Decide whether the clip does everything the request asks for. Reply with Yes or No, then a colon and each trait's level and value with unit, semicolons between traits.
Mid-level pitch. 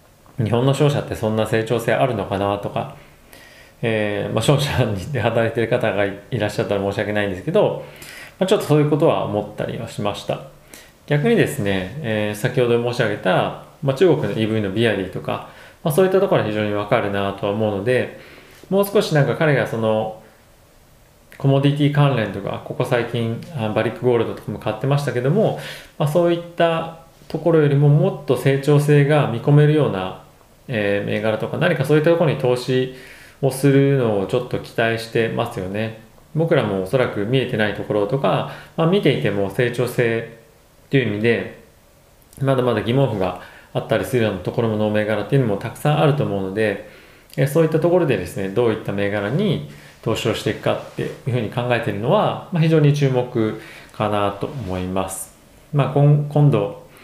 No: low, 120 Hz